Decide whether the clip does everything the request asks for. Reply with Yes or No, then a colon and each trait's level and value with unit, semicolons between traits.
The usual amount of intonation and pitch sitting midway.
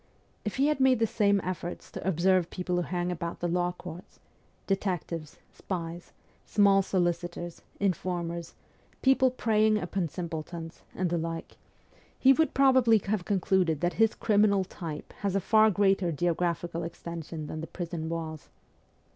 Yes: average, 3.1 semitones; medium, 180 Hz